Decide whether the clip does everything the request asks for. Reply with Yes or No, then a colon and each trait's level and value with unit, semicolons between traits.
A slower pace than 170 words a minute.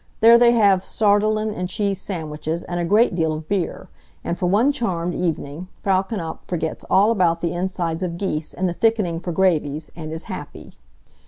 No: average, 185 wpm